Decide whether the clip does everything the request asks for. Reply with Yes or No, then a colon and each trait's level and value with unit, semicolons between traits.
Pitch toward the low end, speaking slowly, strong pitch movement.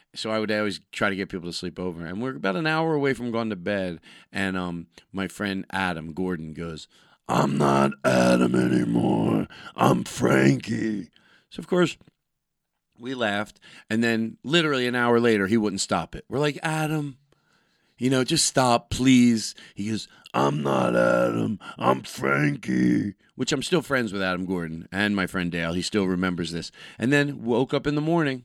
No: low, 100 Hz; average, 180 wpm; wide, 7.0 semitones